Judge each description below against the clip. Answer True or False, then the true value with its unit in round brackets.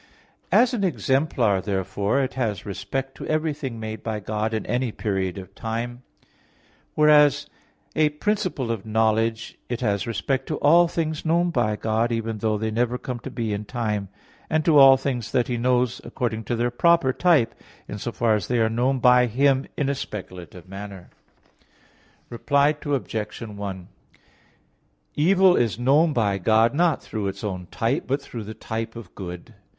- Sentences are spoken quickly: False (170 wpm)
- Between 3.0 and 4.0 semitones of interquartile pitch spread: False (4.4 semitones)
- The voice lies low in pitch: True (115 Hz)